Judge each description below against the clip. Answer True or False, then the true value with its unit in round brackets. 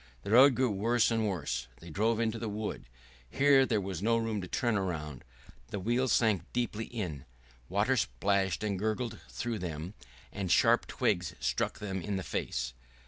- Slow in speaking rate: False (175 wpm)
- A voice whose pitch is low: True (105 Hz)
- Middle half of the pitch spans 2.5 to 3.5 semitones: False (4.0 semitones)